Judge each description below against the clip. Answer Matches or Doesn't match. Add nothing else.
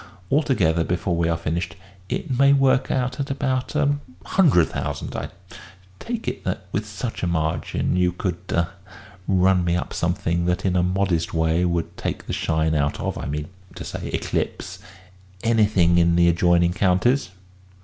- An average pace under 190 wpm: Matches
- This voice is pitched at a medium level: Doesn't match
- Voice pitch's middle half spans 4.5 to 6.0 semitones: Matches